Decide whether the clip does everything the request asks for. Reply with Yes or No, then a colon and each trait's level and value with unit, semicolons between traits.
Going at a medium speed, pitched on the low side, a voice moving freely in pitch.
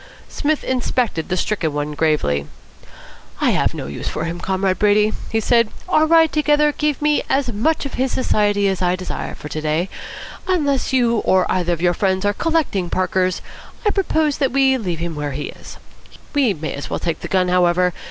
No: average, 195 wpm; high, 200 Hz; wide, 7.8 semitones